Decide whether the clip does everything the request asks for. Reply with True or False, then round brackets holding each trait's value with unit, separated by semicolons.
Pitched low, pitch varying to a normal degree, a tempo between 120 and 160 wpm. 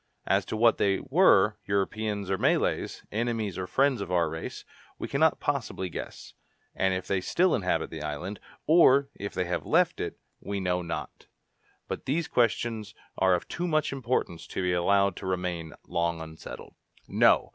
False (100 Hz; 4.6 semitones; 170 wpm)